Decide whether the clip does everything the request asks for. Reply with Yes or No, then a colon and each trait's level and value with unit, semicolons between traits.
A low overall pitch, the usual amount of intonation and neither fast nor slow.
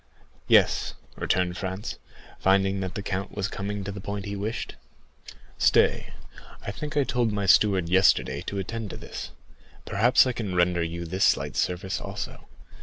No: low, 100 Hz; narrow, 1.8 semitones; average, 165 wpm